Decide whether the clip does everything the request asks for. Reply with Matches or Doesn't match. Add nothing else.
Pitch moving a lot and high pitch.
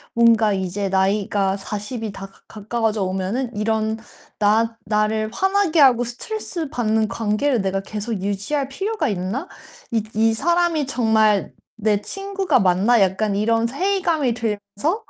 Doesn't match